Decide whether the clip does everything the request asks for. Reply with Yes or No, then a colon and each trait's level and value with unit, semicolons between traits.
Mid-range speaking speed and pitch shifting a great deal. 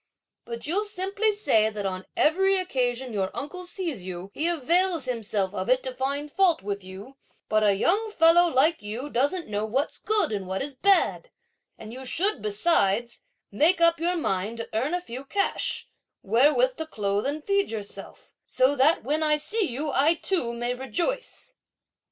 Yes: average, 175 wpm; wide, 8.4 semitones